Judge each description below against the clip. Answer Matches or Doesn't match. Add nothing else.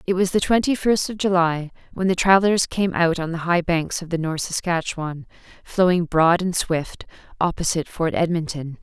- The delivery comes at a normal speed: Matches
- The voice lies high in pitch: Doesn't match